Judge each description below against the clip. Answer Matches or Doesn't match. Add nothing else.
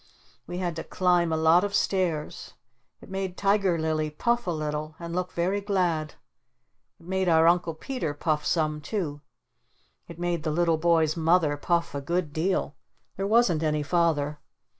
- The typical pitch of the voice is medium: Matches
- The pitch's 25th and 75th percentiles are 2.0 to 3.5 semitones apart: Matches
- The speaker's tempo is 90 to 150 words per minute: Doesn't match